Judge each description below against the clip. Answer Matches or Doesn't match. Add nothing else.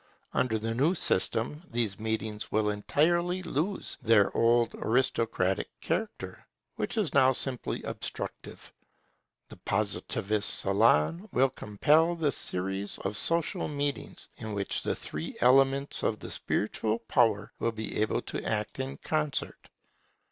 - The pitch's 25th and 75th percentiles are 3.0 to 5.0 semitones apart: Doesn't match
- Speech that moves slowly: Matches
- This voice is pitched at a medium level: Doesn't match